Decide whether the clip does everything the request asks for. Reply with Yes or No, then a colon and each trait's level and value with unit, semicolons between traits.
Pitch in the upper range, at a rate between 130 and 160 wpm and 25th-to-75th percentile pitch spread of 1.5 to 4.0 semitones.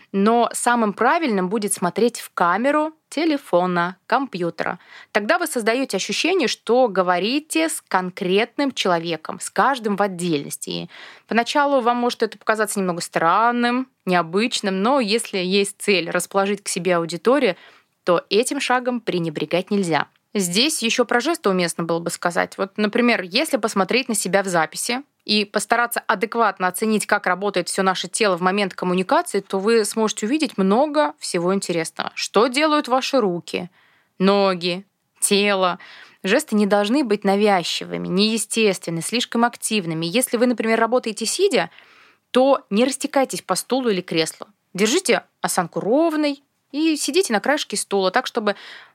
No: high, 210 Hz; average, 140 wpm; average, 5.0 semitones